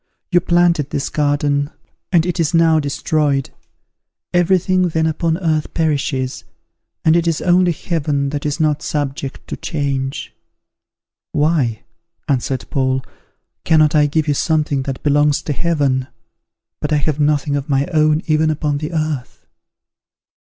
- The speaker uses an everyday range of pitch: No, narrow, 2.2 semitones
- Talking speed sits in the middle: Yes, average, 145 wpm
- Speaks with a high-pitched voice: No, medium, 150 Hz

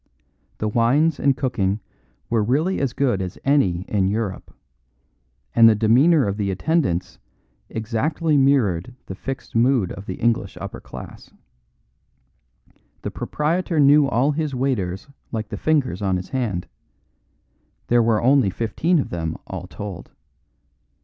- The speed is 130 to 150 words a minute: Yes, slow, 135 wpm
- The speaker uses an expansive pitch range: Yes, wide, 6.2 semitones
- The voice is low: Yes, low, 115 Hz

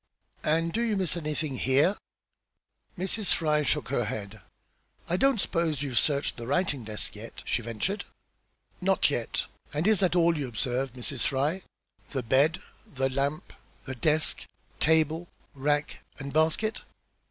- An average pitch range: Yes, average, 4.5 semitones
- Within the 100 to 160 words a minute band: Yes, average, 145 wpm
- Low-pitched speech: No, medium, 150 Hz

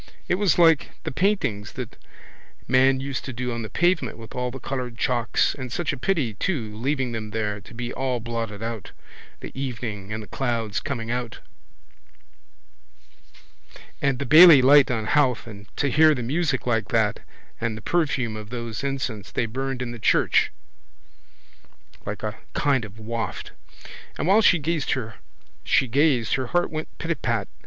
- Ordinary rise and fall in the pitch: Yes, average, 3.8 semitones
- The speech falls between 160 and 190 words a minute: Yes, average, 165 wpm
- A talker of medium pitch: No, low, 125 Hz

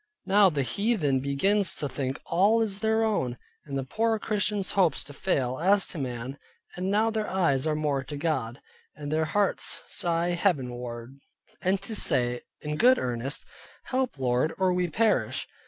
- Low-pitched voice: No, medium, 165 Hz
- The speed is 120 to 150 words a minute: No, average, 170 wpm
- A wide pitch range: Yes, wide, 7.1 semitones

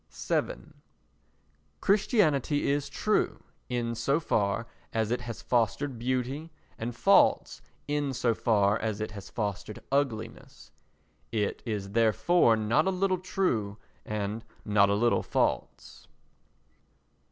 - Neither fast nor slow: No, slow, 120 wpm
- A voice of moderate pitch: No, low, 115 Hz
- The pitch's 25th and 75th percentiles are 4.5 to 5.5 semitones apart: Yes, average, 5.0 semitones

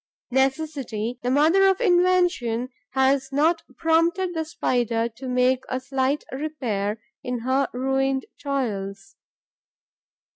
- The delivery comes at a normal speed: No, slow, 110 wpm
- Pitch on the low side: No, very high, 265 Hz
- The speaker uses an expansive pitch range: No, average, 4.2 semitones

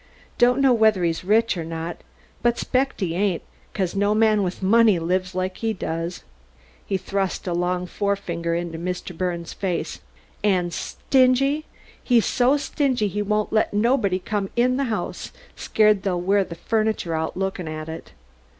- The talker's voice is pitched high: Yes, high, 195 Hz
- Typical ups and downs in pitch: Yes, average, 3.9 semitones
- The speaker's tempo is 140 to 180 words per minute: Yes, average, 165 wpm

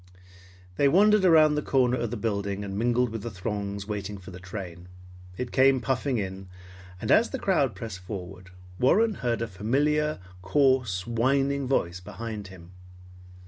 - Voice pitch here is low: Yes, low, 115 Hz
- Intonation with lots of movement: Yes, wide, 5.7 semitones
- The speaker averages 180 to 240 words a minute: No, average, 160 wpm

